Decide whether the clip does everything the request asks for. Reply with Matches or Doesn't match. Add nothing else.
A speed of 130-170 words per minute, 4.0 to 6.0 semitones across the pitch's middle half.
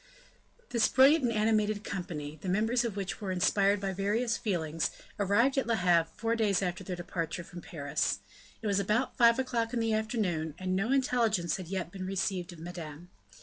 Doesn't match